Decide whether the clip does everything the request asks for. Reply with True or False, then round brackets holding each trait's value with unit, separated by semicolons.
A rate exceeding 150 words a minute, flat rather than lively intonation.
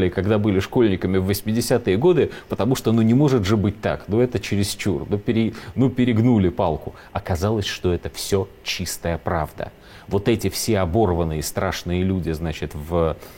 False (160 wpm; 3.8 semitones)